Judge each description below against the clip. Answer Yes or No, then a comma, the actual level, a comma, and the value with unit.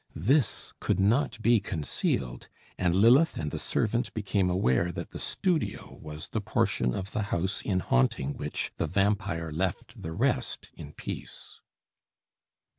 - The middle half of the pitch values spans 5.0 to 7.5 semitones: Yes, wide, 5.4 semitones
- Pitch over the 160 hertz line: No, very low, 95 Hz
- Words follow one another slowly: No, average, 145 wpm